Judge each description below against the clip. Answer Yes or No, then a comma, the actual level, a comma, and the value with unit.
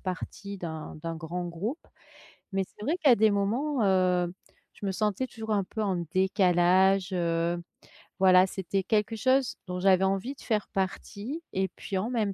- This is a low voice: No, high, 195 Hz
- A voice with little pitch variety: No, average, 3.0 semitones